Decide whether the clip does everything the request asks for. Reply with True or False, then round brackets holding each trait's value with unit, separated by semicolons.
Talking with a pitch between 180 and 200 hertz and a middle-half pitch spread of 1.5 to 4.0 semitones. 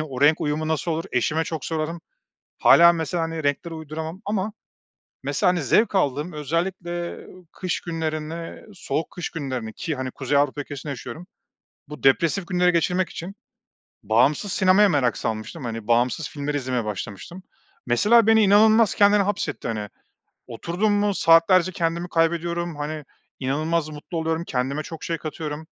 False (160 Hz; 3.7 semitones)